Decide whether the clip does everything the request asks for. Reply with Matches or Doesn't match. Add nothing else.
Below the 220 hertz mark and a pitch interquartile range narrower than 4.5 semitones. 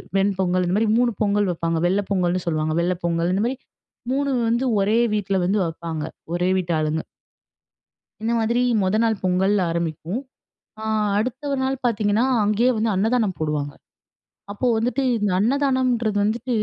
Doesn't match